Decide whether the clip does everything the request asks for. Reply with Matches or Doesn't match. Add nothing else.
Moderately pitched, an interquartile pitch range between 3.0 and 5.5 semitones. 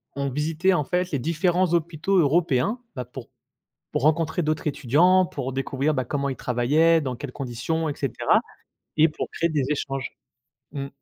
Matches